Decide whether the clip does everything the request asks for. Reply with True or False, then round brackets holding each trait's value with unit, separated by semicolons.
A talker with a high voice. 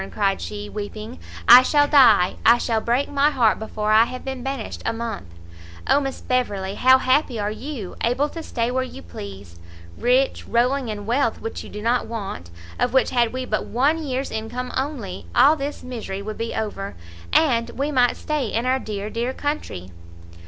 True (240 Hz)